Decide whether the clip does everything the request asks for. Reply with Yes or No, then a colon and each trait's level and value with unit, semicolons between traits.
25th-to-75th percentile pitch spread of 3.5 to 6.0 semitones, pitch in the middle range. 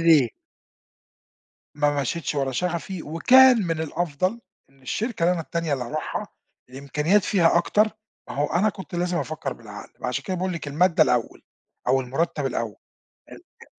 Yes: average, 4.7 semitones; medium, 160 Hz